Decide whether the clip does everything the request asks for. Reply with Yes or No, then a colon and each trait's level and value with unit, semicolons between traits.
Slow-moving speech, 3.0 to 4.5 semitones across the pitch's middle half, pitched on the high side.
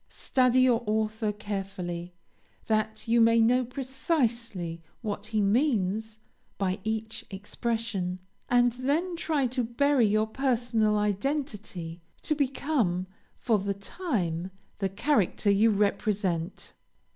Yes: slow, 110 wpm; average, 4.0 semitones; high, 220 Hz